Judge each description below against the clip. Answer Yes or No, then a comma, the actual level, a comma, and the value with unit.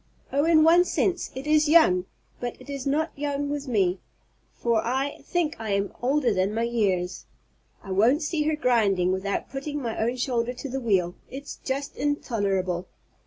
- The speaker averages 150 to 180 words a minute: Yes, average, 175 wpm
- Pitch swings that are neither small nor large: No, wide, 6.3 semitones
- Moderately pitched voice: No, very high, 250 Hz